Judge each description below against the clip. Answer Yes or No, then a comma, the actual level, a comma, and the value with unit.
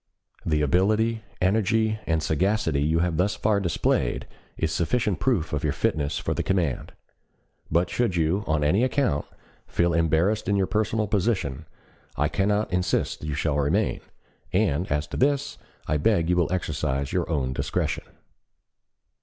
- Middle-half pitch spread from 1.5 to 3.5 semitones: No, wide, 5.4 semitones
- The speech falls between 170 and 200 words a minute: No, average, 155 wpm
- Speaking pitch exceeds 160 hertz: No, very low, 90 Hz